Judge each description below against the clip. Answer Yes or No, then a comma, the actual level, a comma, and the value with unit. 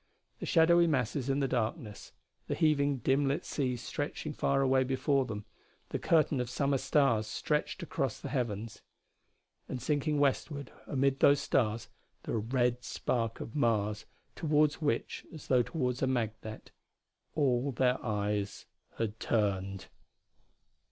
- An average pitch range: Yes, average, 4.0 semitones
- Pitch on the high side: No, low, 130 Hz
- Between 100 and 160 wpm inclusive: Yes, average, 140 wpm